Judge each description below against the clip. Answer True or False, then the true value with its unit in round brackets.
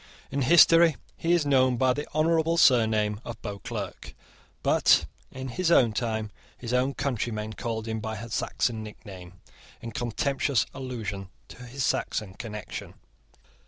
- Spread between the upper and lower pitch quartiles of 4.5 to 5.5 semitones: False (3.9 semitones)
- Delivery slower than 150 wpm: True (140 wpm)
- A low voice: True (120 Hz)